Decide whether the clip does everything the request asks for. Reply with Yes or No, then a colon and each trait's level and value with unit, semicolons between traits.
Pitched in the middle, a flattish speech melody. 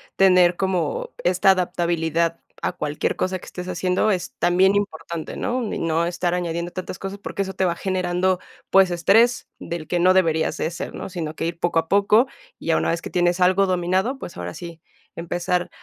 Yes: medium, 180 Hz; narrow, 1.9 semitones